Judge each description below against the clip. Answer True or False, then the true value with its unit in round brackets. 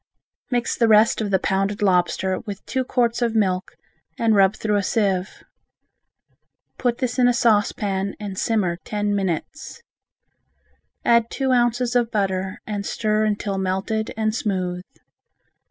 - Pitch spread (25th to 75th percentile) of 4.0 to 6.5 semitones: False (3.4 semitones)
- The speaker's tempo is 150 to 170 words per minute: False (140 wpm)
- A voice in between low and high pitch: False (210 Hz)